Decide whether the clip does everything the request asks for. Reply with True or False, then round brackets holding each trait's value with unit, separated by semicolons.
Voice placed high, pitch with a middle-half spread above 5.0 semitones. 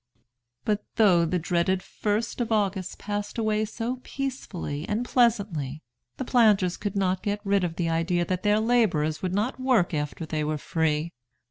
False (195 Hz; 4.7 semitones)